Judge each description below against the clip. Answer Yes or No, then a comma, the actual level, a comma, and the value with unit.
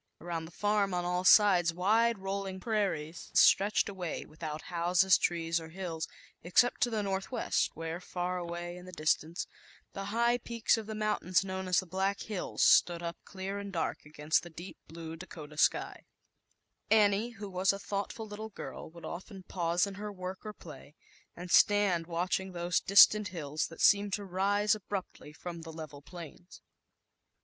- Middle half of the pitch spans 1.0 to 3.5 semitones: Yes, average, 3.1 semitones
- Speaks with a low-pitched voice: No, medium, 185 Hz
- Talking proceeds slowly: No, average, 150 wpm